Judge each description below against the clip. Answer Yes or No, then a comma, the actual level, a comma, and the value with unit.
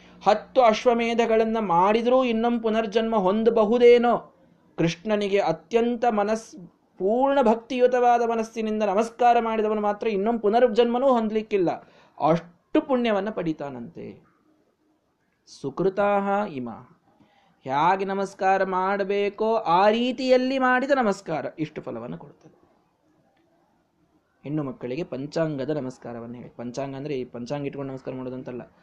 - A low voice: No, high, 205 Hz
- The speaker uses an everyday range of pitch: No, wide, 6.7 semitones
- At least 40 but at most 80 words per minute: No, average, 90 wpm